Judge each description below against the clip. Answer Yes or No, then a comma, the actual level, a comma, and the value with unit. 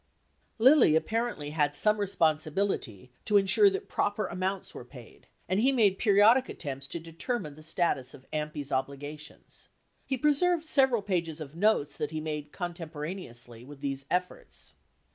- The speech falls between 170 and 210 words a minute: No, average, 150 wpm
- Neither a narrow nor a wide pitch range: No, wide, 6.3 semitones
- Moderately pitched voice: Yes, medium, 165 Hz